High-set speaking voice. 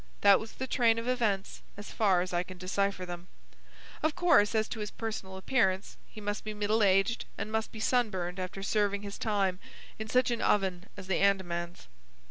Yes: high, 205 Hz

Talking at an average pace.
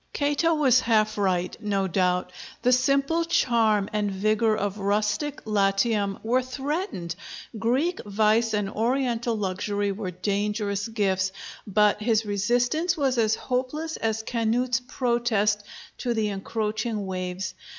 No: slow, 125 wpm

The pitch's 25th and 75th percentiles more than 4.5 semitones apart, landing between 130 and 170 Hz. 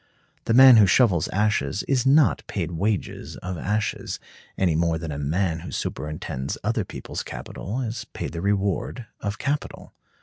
No: average, 5.2 semitones; low, 100 Hz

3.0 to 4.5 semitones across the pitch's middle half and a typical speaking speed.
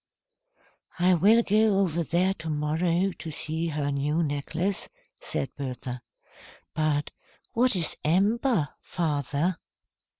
No: average, 4.2 semitones; slow, 110 wpm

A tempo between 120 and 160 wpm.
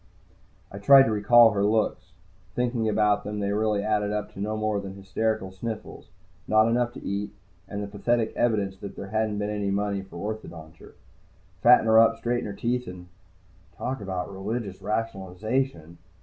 No: average, 170 wpm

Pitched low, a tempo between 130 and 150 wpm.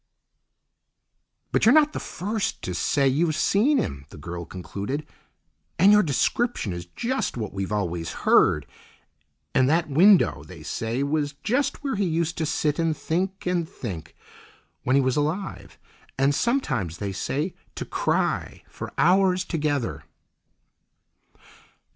No: medium, 150 Hz; average, 140 wpm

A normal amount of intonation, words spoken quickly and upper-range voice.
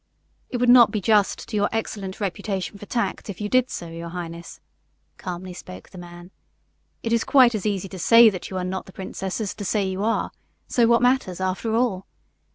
Yes: average, 3.6 semitones; fast, 215 wpm; high, 200 Hz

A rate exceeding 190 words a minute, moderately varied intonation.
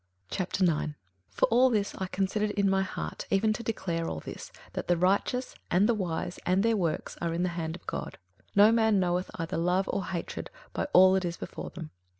Yes: fast, 205 wpm; average, 3.2 semitones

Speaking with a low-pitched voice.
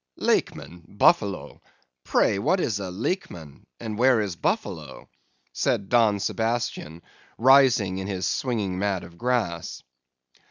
Yes: low, 100 Hz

